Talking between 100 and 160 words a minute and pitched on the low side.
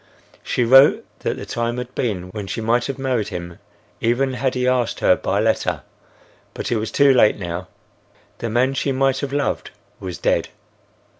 No: average, 180 wpm; low, 120 Hz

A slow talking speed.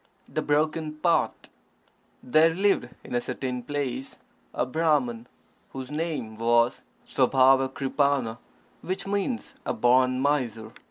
Yes: slow, 110 wpm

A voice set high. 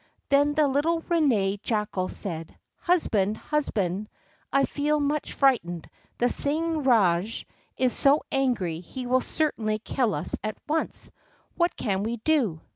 Yes: very high, 250 Hz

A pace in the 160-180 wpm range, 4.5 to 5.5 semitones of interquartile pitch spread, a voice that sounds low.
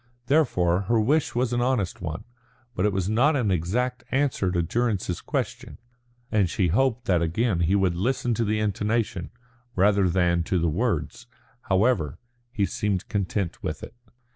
Yes: average, 165 wpm; average, 5.2 semitones; low, 100 Hz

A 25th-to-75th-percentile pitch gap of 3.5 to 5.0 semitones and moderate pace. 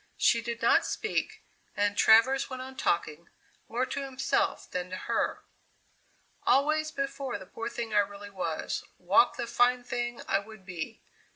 Yes: average, 4.6 semitones; average, 160 wpm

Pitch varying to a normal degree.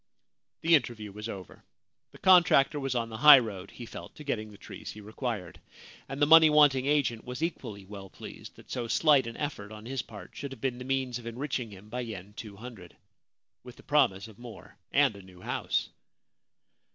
Yes: average, 4.5 semitones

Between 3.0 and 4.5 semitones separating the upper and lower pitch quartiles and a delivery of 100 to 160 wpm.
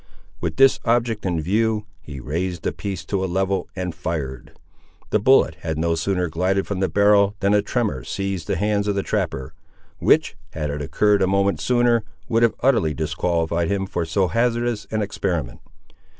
No: average, 4.1 semitones; average, 180 wpm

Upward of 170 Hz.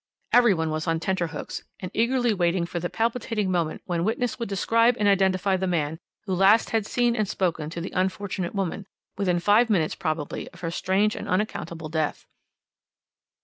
Yes: high, 190 Hz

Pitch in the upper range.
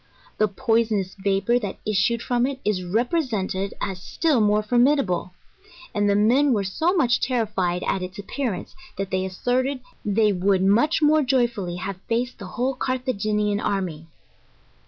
Yes: high, 210 Hz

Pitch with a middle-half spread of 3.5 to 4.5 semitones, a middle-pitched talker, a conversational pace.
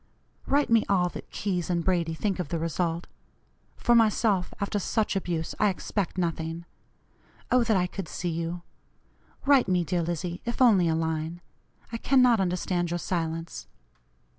Yes: average, 3.8 semitones; medium, 180 Hz; average, 160 wpm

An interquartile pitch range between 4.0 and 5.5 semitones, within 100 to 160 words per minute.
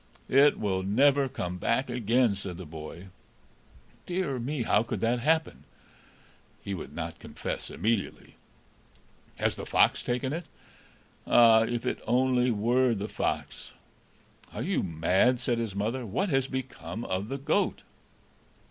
Yes: average, 4.8 semitones; average, 140 wpm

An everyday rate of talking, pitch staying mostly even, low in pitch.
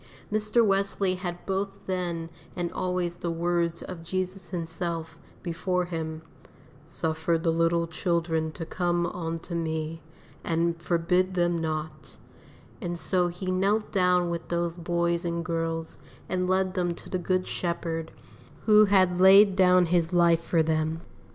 No: average, 145 wpm; narrow, 1.8 semitones; medium, 175 Hz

